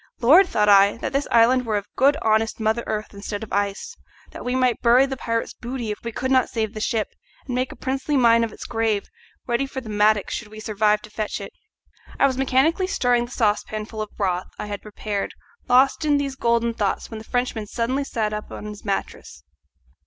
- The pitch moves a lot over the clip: No, average, 3.3 semitones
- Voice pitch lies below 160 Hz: No, high, 230 Hz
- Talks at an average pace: No, fast, 220 wpm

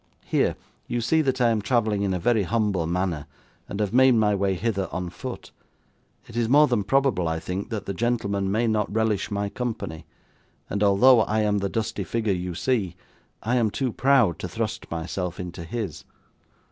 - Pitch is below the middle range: Yes, low, 105 Hz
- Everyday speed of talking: Yes, average, 190 wpm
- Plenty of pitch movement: No, average, 3.9 semitones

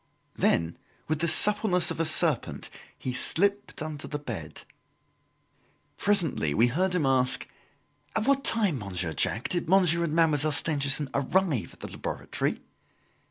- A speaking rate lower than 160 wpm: Yes, average, 140 wpm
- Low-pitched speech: No, medium, 155 Hz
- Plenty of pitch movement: Yes, wide, 5.8 semitones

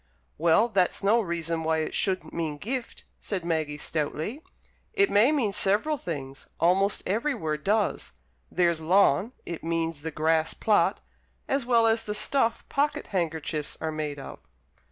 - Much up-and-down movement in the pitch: Yes, wide, 5.8 semitones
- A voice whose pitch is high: No, medium, 175 Hz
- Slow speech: No, average, 155 wpm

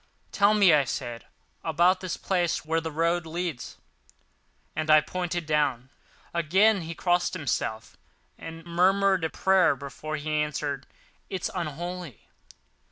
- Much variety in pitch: No, average, 3.0 semitones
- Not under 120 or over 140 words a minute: Yes, slow, 135 wpm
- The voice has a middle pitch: Yes, medium, 165 Hz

